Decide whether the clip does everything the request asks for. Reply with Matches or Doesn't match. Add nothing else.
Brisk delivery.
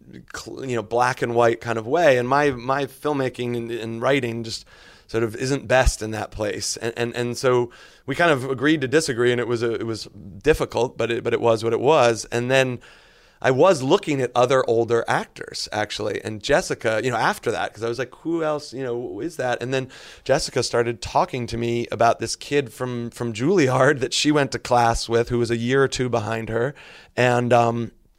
Matches